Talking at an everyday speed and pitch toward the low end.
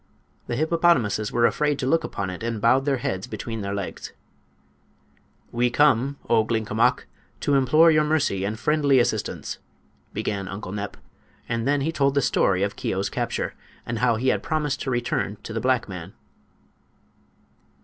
Yes: average, 165 wpm; low, 120 Hz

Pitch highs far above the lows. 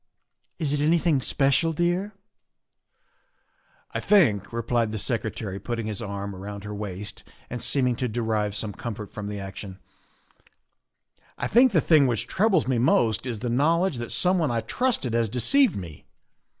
Yes: wide, 6.8 semitones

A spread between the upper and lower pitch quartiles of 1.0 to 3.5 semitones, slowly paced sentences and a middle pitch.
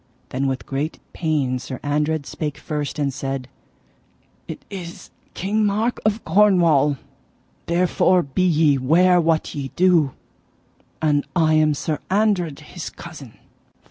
No: average, 4.1 semitones; slow, 130 wpm; medium, 155 Hz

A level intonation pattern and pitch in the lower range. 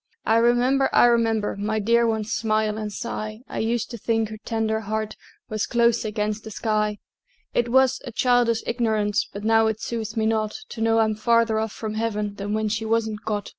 No: narrow, 1.3 semitones; high, 220 Hz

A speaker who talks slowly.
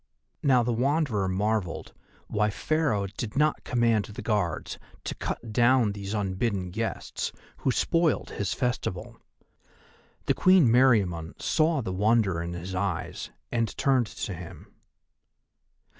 Yes: slow, 130 wpm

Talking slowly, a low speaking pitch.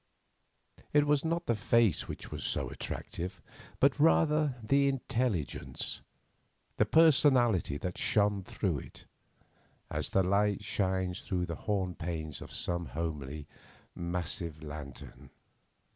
Yes: slow, 120 wpm; very low, 95 Hz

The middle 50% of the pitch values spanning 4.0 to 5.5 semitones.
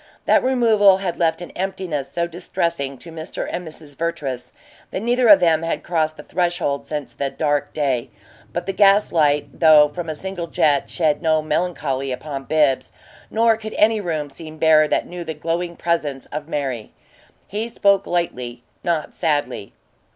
No: average, 3.3 semitones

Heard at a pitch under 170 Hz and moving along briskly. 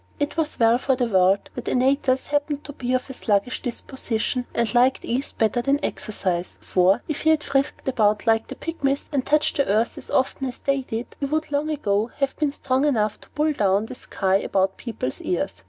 No: very high, 255 Hz; fast, 210 wpm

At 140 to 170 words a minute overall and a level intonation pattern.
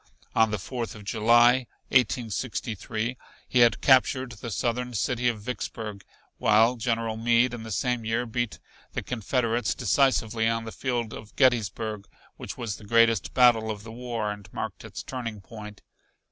Yes: average, 160 wpm; narrow, 2.1 semitones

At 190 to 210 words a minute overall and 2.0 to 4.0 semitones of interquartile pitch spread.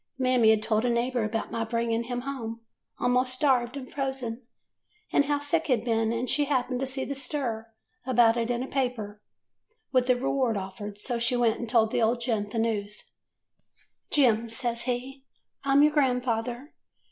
Yes: average, 195 wpm; narrow, 2.6 semitones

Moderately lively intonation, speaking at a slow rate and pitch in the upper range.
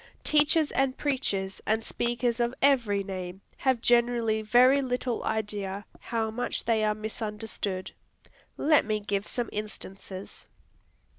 Yes: average, 3.2 semitones; slow, 125 wpm; high, 220 Hz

